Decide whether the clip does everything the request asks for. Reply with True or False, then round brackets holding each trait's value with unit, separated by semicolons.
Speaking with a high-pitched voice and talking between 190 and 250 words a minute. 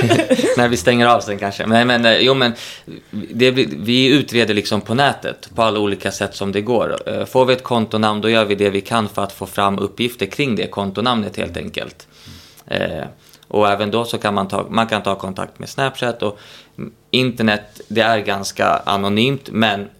False (110 Hz; 195 wpm)